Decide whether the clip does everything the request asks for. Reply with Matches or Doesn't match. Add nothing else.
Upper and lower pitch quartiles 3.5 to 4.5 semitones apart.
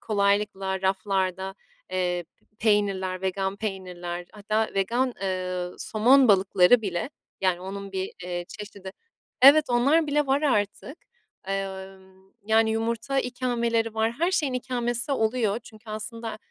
Matches